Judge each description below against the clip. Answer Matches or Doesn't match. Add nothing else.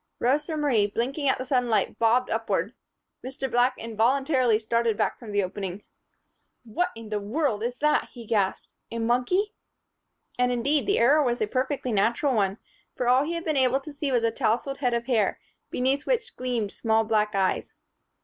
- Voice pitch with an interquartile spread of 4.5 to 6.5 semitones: Doesn't match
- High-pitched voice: Matches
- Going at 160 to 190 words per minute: Matches